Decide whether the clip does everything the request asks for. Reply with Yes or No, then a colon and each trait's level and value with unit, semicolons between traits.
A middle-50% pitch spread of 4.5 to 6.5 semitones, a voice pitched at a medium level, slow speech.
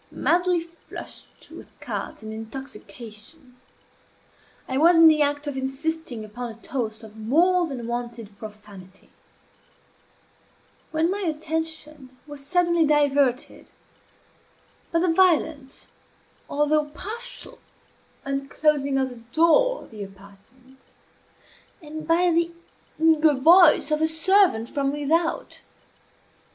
No: average, 4.8 semitones; very high, 295 Hz; slow, 110 wpm